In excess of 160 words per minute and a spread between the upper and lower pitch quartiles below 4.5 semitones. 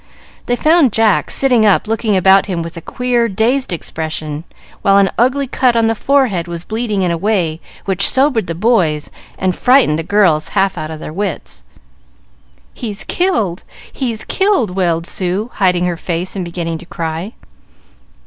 No: average, 170 wpm; wide, 5.5 semitones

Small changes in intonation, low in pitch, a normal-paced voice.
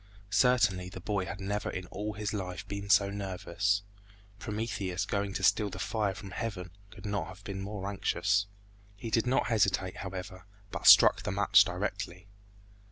Yes: narrow, 1.9 semitones; low, 100 Hz; average, 165 wpm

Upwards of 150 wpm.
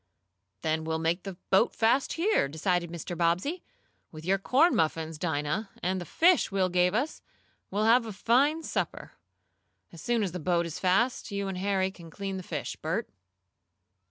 Yes: average, 175 wpm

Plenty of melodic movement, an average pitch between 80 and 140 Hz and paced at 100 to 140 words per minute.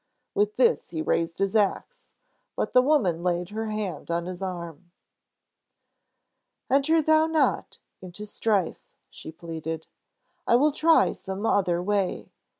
No: wide, 5.7 semitones; high, 195 Hz; slow, 135 wpm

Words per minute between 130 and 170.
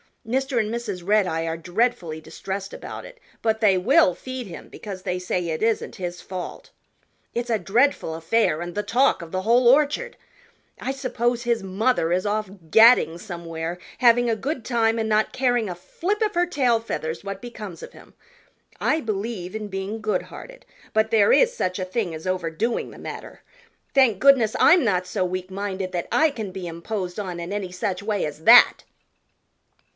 No: average, 180 wpm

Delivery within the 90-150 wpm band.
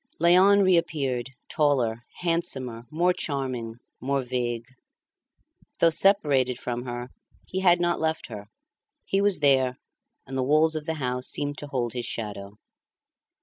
Yes: average, 140 wpm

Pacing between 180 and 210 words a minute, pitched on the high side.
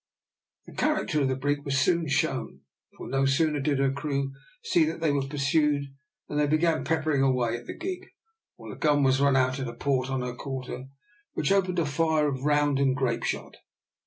No: fast, 205 wpm; medium, 140 Hz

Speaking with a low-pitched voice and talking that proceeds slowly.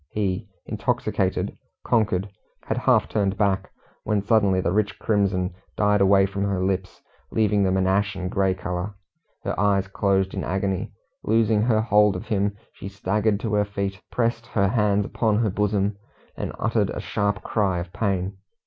No: low, 100 Hz; average, 165 wpm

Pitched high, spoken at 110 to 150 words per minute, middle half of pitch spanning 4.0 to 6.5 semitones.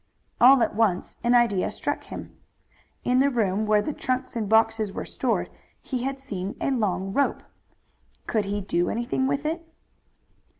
No: high, 230 Hz; average, 165 wpm; average, 4.4 semitones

